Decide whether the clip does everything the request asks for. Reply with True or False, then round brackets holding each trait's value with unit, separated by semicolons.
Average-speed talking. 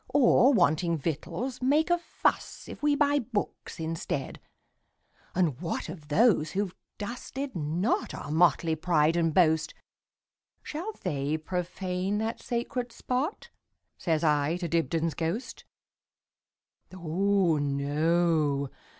False (100 wpm)